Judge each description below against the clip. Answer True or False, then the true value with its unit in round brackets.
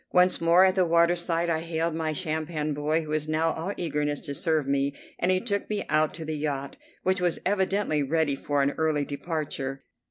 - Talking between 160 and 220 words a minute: True (200 wpm)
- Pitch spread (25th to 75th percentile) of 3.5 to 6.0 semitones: False (2.7 semitones)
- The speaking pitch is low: False (160 Hz)